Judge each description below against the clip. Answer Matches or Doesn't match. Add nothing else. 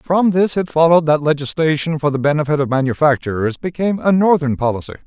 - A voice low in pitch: Doesn't match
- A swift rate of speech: Doesn't match